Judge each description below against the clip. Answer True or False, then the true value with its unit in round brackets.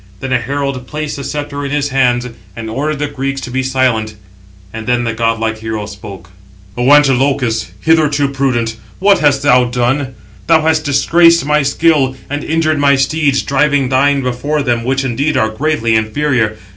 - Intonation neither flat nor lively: True (3.3 semitones)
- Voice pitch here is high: False (135 Hz)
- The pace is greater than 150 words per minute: True (170 wpm)